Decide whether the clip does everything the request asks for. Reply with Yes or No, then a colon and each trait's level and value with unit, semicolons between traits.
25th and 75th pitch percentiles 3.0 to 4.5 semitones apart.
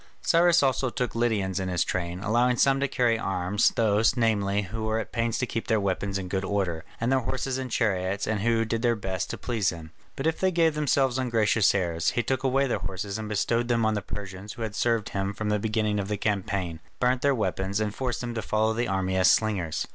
Yes: average, 3.7 semitones